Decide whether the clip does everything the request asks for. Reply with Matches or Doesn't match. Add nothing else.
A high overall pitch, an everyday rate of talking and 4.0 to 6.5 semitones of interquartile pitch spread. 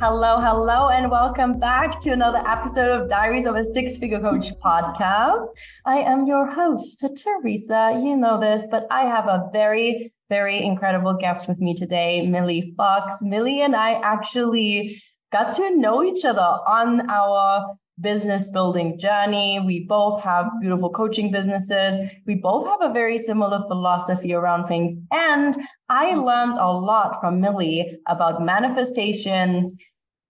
Matches